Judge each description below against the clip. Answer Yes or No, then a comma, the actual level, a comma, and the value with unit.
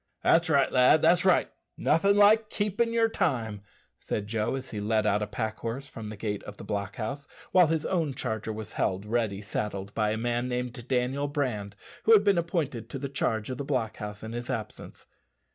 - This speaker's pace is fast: Yes, fast, 210 wpm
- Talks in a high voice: No, low, 120 Hz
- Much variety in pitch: Yes, wide, 6.0 semitones